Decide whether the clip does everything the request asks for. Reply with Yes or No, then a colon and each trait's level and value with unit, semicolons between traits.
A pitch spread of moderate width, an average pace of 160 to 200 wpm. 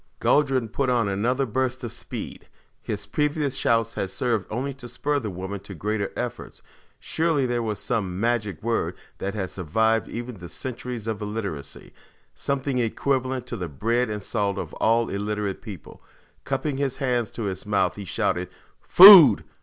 Yes: average, 4.2 semitones; average, 165 wpm